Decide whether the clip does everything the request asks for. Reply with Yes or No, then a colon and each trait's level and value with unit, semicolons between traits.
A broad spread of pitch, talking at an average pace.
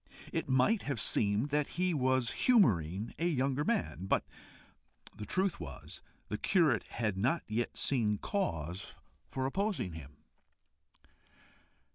No: wide, 8.4 semitones; slow, 125 wpm